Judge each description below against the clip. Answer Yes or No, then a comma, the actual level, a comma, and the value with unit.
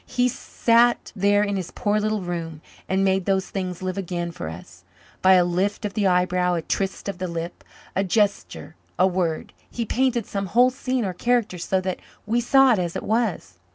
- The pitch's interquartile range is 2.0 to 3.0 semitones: No, average, 3.4 semitones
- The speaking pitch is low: No, high, 190 Hz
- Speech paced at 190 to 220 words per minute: Yes, average, 200 wpm